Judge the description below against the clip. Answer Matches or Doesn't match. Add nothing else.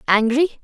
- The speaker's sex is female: Matches